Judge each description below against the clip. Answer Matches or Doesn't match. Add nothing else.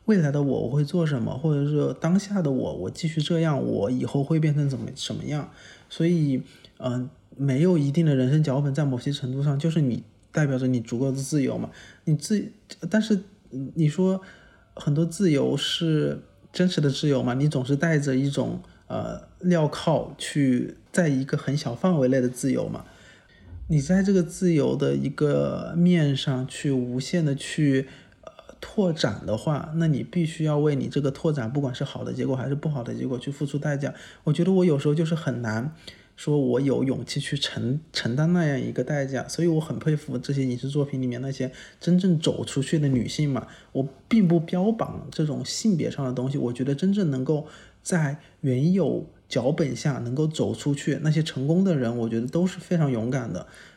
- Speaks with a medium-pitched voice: Matches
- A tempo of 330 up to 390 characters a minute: Doesn't match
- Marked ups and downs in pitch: Doesn't match